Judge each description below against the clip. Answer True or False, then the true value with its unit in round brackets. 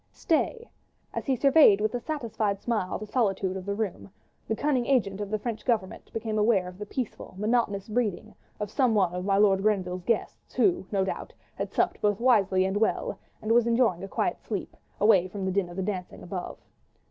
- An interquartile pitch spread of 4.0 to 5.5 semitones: False (3.4 semitones)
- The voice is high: True (210 Hz)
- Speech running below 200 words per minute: False (205 wpm)